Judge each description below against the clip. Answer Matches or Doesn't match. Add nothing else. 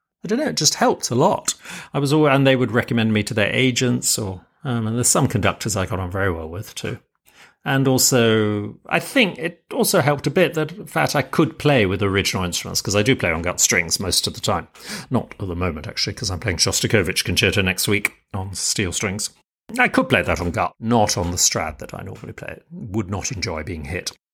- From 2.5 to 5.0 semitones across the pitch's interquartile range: Doesn't match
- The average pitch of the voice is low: Matches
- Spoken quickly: Matches